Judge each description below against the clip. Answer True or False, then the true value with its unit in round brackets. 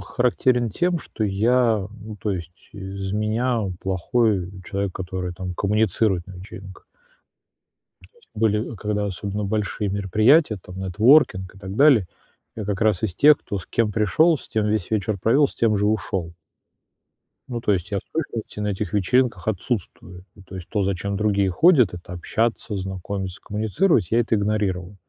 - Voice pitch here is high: False (105 Hz)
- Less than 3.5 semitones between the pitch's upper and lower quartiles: True (2.9 semitones)